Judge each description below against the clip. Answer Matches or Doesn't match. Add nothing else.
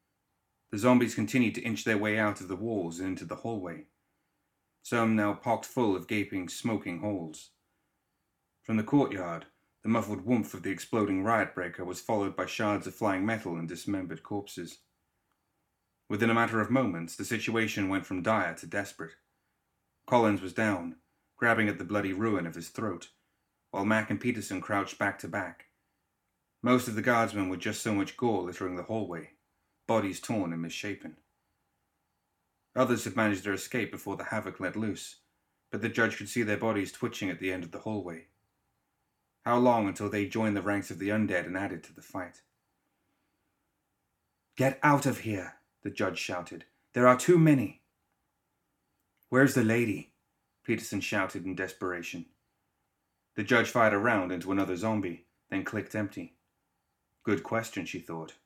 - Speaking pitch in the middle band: Doesn't match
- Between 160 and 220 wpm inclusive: Matches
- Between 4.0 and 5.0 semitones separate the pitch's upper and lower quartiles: Doesn't match